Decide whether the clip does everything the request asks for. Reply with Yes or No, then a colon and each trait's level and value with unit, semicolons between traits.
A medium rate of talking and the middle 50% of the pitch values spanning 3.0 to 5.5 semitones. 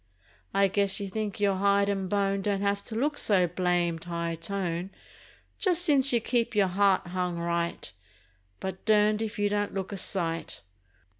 No: average, 170 wpm; narrow, 2.6 semitones